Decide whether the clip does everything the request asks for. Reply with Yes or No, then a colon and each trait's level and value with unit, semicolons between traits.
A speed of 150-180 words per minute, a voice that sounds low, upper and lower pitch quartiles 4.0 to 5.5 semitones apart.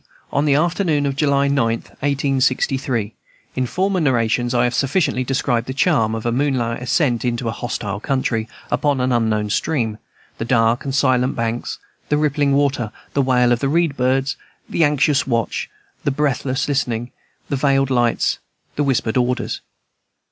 No: average, 160 wpm; low, 130 Hz; average, 2.9 semitones